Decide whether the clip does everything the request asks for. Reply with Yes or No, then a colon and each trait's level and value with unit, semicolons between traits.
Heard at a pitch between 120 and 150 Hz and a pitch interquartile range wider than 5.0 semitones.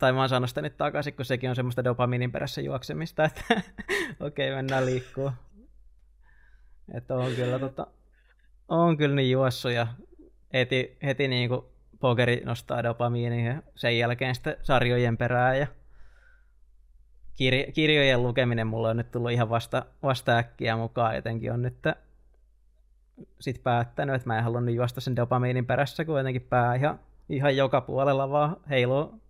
No: low, 125 Hz; narrow, 2.4 semitones